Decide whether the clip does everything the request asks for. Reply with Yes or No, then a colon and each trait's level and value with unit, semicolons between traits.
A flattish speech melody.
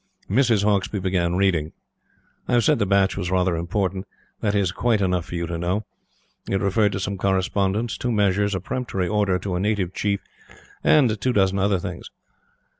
Yes: narrow, 2.1 semitones